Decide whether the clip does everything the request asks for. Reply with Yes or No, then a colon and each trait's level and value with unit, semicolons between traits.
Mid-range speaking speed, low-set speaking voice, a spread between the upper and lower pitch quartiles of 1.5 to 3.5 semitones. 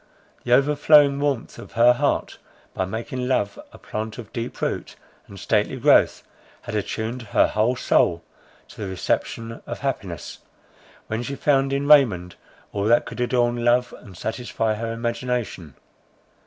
Yes: average, 150 wpm; low, 120 Hz; average, 2.8 semitones